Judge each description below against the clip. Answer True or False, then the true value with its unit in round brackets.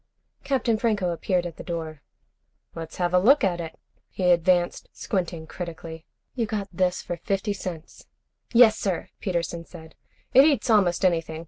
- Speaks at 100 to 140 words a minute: False (155 wpm)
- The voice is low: False (180 Hz)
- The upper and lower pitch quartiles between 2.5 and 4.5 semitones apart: True (3.3 semitones)